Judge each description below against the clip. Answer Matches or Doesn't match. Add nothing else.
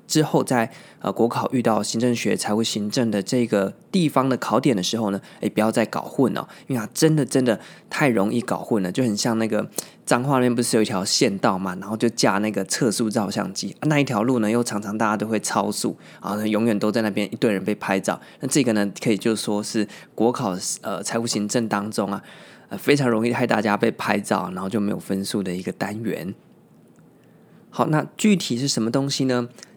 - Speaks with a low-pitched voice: Matches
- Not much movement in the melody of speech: Doesn't match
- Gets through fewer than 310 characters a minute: Doesn't match